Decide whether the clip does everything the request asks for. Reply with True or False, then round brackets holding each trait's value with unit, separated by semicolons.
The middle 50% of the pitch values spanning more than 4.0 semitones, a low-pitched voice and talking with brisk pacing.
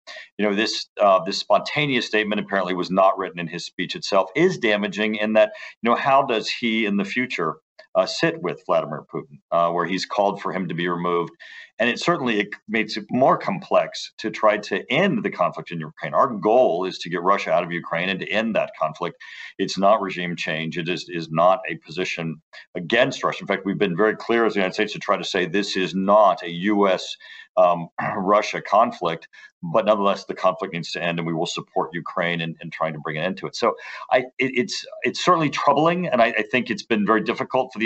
True (4.6 semitones; 100 Hz; 225 wpm)